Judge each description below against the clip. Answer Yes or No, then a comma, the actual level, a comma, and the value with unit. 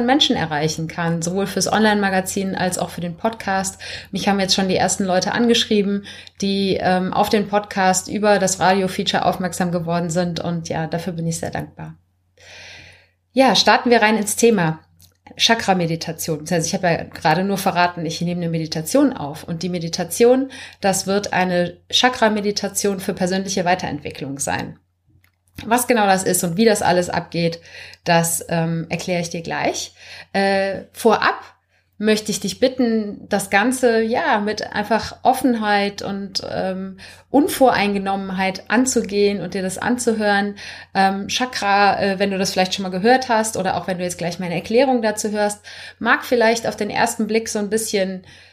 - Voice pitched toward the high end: Yes, high, 195 Hz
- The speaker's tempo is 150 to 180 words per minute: Yes, average, 165 wpm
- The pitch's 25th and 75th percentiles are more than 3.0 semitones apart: Yes, average, 3.6 semitones